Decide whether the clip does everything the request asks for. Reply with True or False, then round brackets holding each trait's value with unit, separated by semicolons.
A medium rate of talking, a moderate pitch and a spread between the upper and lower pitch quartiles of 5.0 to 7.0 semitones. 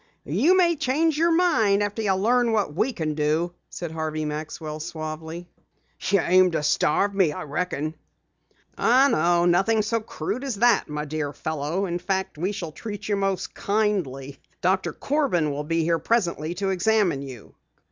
True (170 wpm; 180 Hz; 5.6 semitones)